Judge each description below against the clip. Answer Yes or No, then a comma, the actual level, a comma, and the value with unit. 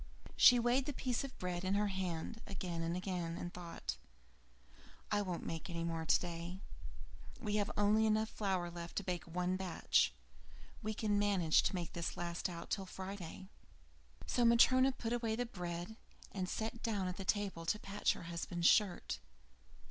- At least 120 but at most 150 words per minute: No, average, 170 wpm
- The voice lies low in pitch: No, high, 190 Hz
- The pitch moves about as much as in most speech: Yes, average, 3.7 semitones